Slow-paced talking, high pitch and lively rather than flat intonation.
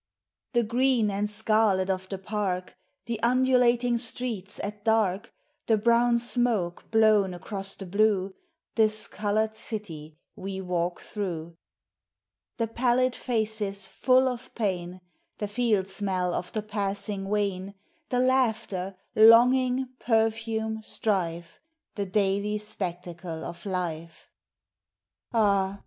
No: slow, 120 wpm; high, 210 Hz; average, 3.2 semitones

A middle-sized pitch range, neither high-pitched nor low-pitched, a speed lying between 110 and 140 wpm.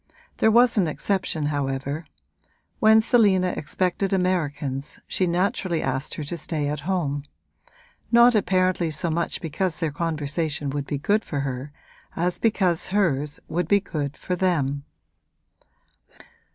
Yes: average, 4.5 semitones; medium, 170 Hz; slow, 135 wpm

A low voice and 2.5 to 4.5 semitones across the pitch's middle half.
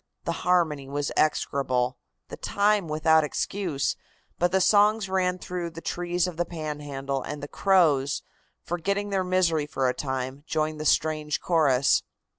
No: medium, 160 Hz; average, 4.0 semitones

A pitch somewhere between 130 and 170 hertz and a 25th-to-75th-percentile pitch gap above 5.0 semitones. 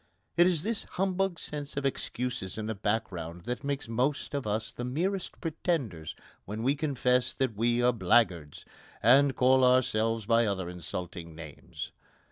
No: low, 120 Hz; wide, 5.4 semitones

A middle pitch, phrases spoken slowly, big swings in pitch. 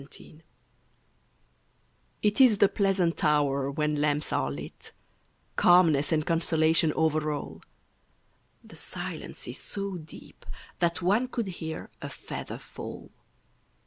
No: medium, 160 Hz; slow, 115 wpm; average, 3.6 semitones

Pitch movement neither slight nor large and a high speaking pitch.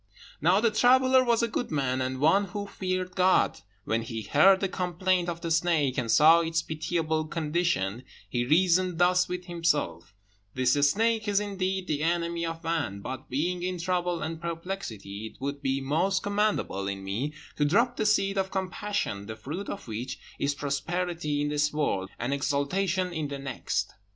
No: average, 4.8 semitones; medium, 165 Hz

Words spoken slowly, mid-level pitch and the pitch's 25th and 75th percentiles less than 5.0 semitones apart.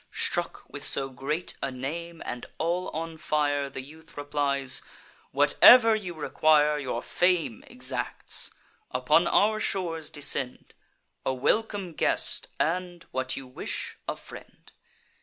Yes: slow, 125 wpm; medium, 150 Hz; average, 4.0 semitones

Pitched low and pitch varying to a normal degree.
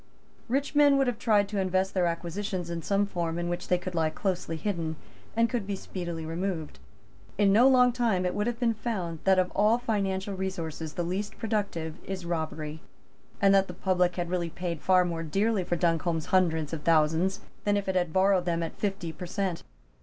No: medium, 185 Hz; average, 3.2 semitones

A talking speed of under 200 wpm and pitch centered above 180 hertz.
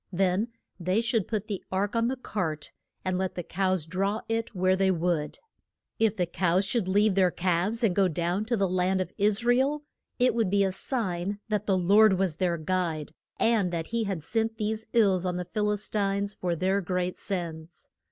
No: fast, 205 wpm; high, 190 Hz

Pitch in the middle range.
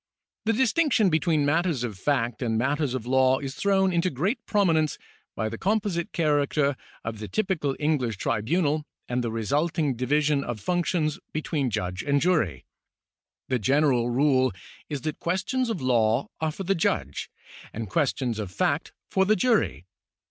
Yes: medium, 145 Hz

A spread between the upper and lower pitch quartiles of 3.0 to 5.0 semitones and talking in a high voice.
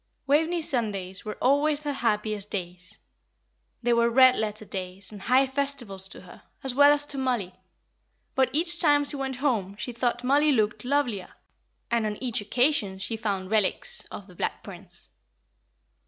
No: wide, 5.4 semitones; high, 235 Hz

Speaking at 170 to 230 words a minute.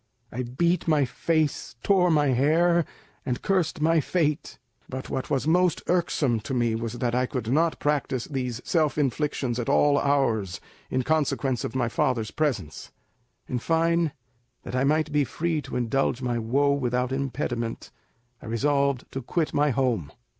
No: average, 160 wpm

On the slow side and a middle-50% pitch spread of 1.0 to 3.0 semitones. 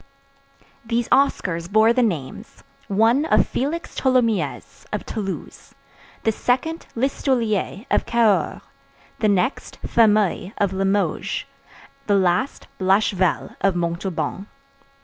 No: slow, 105 wpm; average, 4.0 semitones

